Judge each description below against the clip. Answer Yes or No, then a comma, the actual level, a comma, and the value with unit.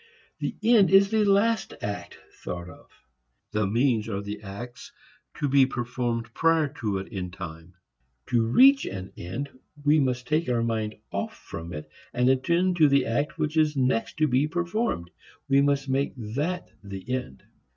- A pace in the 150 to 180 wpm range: Yes, average, 170 wpm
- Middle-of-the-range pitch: No, low, 125 Hz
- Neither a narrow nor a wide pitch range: No, wide, 6.4 semitones